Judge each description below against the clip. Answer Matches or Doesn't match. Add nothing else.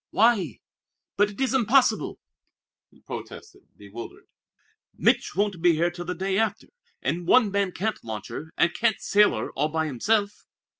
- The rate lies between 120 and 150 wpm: Doesn't match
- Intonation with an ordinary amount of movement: Matches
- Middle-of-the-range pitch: Doesn't match